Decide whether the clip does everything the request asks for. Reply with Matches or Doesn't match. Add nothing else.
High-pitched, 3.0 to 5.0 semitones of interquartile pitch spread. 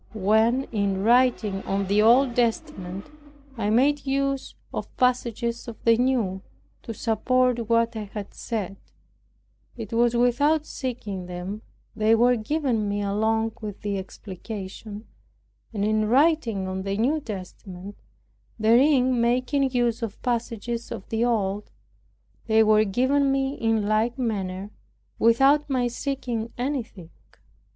Matches